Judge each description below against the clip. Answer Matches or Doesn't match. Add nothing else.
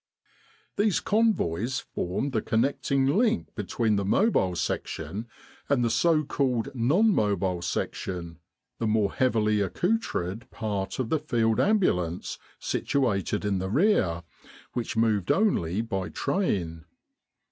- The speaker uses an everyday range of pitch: Doesn't match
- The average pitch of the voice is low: Matches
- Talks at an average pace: Doesn't match